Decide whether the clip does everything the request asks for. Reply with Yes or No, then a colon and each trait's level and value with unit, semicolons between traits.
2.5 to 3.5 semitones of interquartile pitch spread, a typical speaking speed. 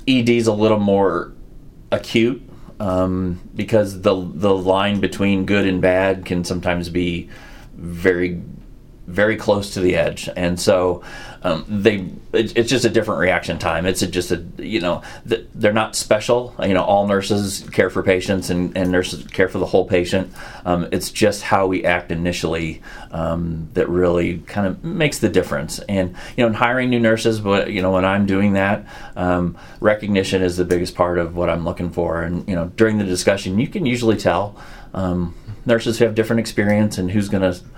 Yes: average, 3.0 semitones; average, 190 wpm